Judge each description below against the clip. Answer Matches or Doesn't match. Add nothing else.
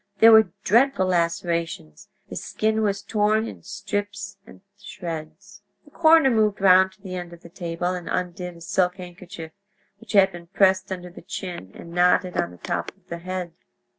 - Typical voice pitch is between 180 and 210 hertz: Matches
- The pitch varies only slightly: Doesn't match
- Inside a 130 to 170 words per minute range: Doesn't match